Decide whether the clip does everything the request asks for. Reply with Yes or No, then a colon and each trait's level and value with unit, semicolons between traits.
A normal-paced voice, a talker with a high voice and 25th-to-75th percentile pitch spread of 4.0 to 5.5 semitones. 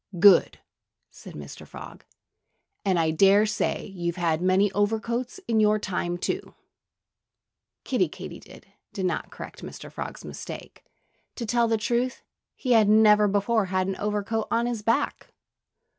No: average, 145 wpm; high, 210 Hz; average, 3.1 semitones